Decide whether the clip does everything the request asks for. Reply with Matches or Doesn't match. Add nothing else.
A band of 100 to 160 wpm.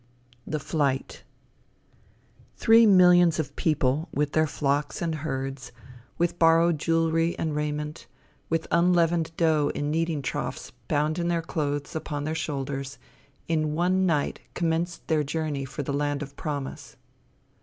Matches